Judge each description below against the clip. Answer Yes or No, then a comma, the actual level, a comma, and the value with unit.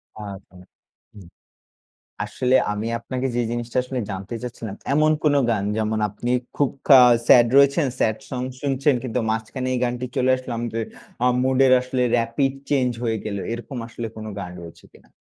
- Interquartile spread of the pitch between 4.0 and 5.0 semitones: No, average, 3.1 semitones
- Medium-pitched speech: No, low, 120 Hz